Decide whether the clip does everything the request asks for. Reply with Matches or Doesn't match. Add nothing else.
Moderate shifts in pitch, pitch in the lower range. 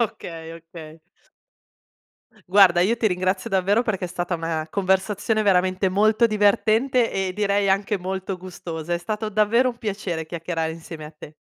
Doesn't match